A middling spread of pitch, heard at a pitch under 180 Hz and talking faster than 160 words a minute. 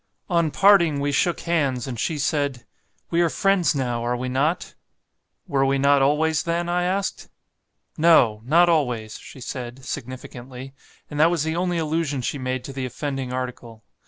Yes: average, 4.6 semitones; medium, 140 Hz; average, 170 wpm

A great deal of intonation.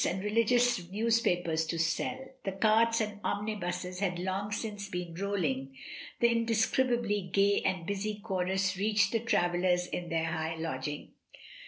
No: average, 3.6 semitones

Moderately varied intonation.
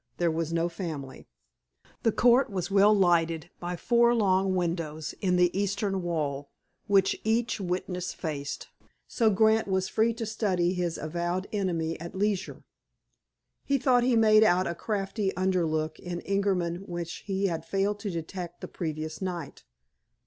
Yes: average, 3.2 semitones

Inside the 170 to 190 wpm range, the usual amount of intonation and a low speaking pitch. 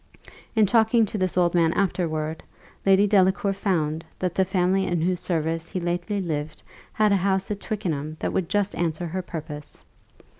No: average, 175 wpm; average, 3.2 semitones; medium, 180 Hz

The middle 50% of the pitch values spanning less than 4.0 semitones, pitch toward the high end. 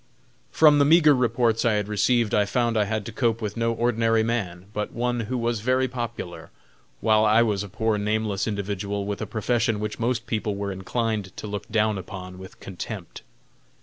No: narrow, 2.5 semitones; low, 110 Hz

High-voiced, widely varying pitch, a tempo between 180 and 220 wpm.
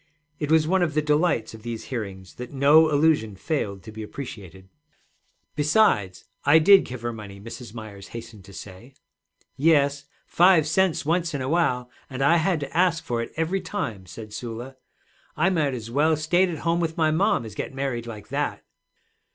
No: medium, 140 Hz; wide, 6.2 semitones; average, 185 wpm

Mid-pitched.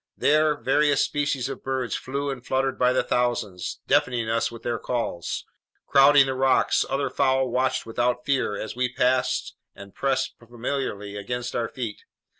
No: low, 125 Hz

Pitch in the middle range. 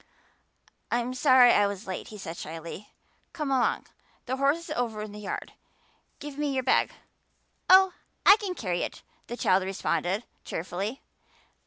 No: high, 240 Hz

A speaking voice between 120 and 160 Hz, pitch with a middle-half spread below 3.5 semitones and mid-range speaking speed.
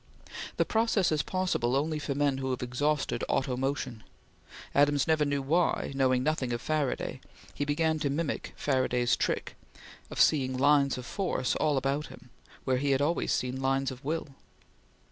Yes: medium, 140 Hz; average, 2.7 semitones; average, 165 wpm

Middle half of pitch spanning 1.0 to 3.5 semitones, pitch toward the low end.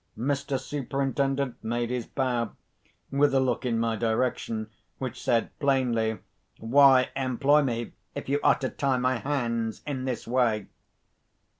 Yes: average, 2.8 semitones; low, 130 Hz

